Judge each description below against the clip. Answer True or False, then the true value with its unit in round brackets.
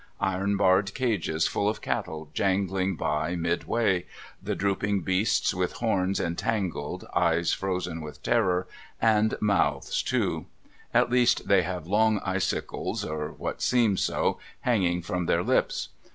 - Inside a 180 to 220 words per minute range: False (135 wpm)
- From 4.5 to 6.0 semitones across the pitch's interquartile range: False (2.9 semitones)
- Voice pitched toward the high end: False (95 Hz)